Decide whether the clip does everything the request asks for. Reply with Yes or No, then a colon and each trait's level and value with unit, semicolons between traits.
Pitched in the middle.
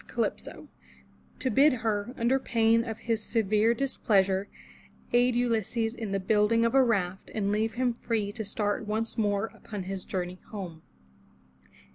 No: high, 220 Hz